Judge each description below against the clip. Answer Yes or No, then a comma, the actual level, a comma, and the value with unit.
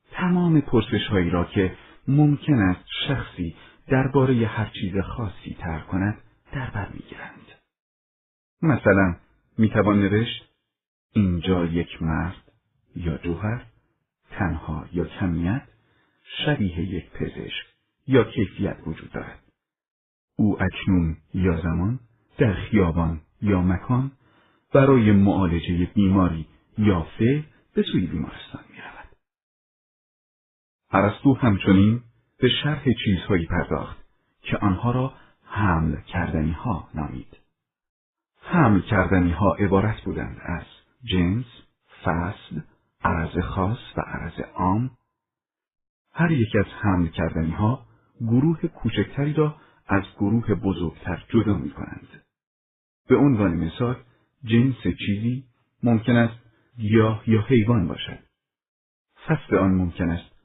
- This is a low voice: Yes, low, 105 Hz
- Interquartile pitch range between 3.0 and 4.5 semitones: No, average, 5.2 semitones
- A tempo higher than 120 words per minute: No, average, 110 wpm